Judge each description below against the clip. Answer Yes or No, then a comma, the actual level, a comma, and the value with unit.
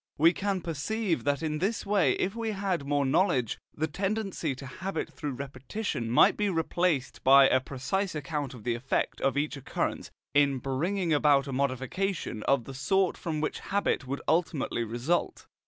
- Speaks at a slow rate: No, average, 170 wpm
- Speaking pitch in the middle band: Yes, medium, 150 Hz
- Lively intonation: Yes, wide, 5.8 semitones